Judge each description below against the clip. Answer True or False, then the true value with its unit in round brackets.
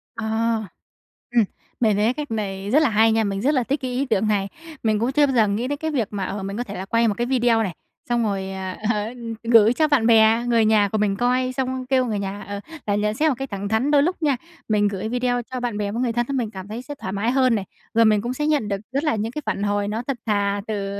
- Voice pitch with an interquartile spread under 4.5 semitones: True (3.8 semitones)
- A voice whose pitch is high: True (225 Hz)